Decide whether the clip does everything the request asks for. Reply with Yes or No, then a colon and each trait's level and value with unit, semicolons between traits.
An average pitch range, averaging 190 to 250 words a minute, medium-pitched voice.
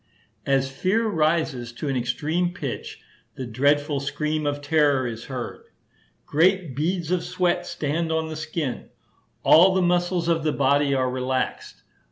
No: average, 4.0 semitones; average, 150 wpm; medium, 150 Hz